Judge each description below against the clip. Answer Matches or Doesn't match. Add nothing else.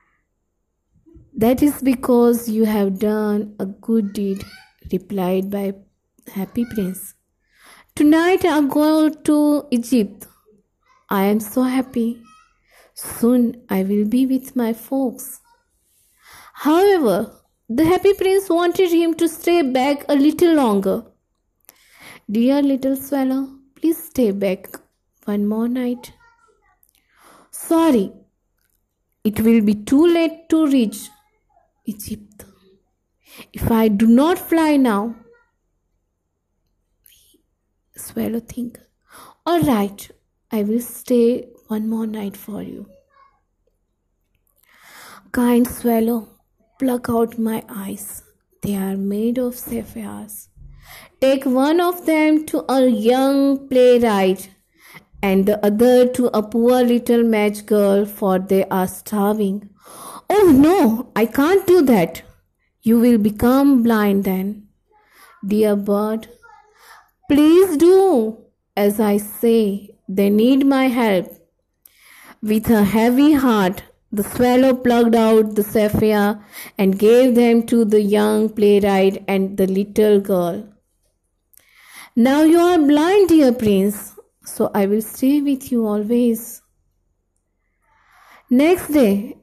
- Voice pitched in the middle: Doesn't match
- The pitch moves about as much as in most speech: Matches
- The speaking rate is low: Matches